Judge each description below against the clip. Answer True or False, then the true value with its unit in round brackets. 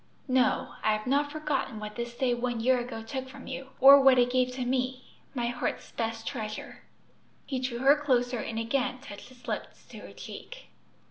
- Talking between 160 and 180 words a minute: False (195 wpm)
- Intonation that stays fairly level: True (2.0 semitones)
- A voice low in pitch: False (255 Hz)